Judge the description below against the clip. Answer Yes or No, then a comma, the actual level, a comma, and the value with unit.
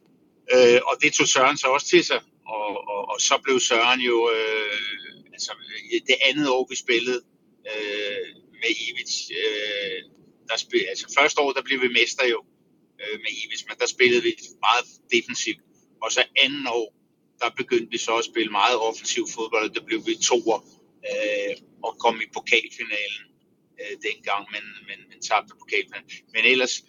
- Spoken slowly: No, average, 175 wpm